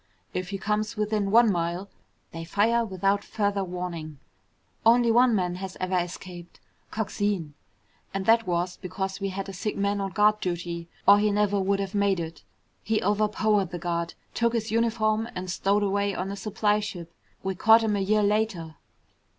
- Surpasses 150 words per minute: Yes, average, 175 wpm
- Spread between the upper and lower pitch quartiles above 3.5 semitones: No, average, 2.8 semitones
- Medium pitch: No, high, 200 Hz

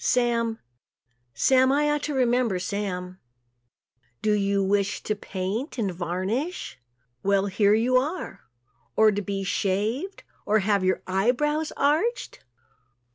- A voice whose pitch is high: Yes, high, 215 Hz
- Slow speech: Yes, slow, 130 wpm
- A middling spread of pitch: Yes, average, 4.8 semitones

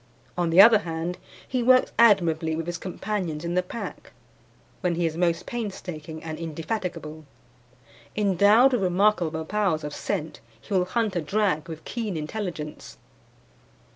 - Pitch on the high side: No, medium, 180 Hz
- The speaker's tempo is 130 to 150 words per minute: Yes, average, 145 wpm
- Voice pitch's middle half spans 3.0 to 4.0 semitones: No, average, 4.4 semitones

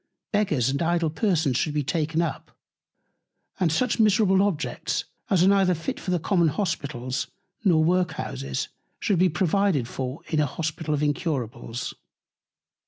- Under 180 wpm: Yes, average, 150 wpm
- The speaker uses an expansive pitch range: No, average, 4.2 semitones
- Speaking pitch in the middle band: Yes, medium, 165 Hz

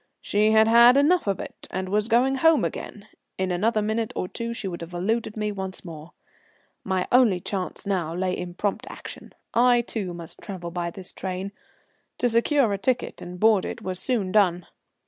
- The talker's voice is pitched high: Yes, high, 200 Hz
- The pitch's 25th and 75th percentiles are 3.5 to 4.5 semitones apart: Yes, average, 4.2 semitones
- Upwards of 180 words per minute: Yes, average, 190 wpm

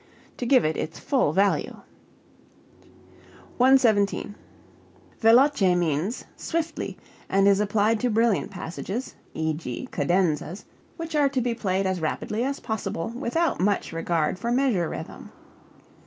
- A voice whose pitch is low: No, high, 205 Hz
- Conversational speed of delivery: No, slow, 125 wpm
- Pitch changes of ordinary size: No, wide, 5.9 semitones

